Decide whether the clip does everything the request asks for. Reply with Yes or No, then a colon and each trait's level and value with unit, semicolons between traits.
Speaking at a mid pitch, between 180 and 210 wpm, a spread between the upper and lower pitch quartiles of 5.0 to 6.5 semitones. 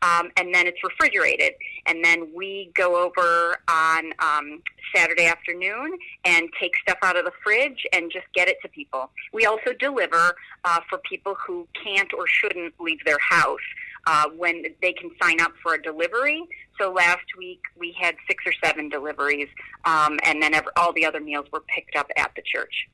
No: medium, 175 Hz; average, 185 wpm; average, 3.4 semitones